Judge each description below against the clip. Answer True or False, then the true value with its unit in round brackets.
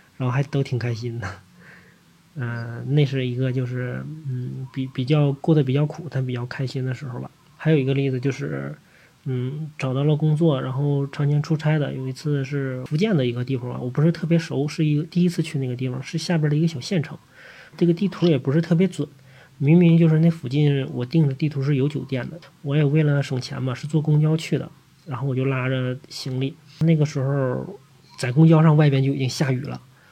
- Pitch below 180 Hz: True (140 Hz)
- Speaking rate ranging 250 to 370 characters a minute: True (310 characters per minute)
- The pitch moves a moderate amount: True (3.0 semitones)